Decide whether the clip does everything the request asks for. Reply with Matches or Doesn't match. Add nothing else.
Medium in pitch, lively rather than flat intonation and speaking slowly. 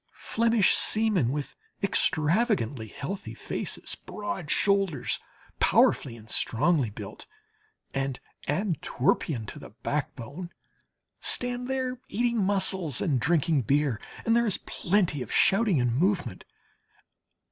Matches